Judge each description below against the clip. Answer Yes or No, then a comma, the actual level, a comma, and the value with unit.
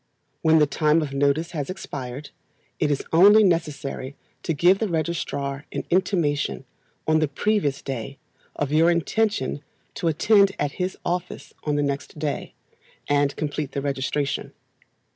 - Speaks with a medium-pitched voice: Yes, medium, 150 Hz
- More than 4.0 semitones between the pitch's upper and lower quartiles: No, average, 3.4 semitones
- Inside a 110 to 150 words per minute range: Yes, average, 145 wpm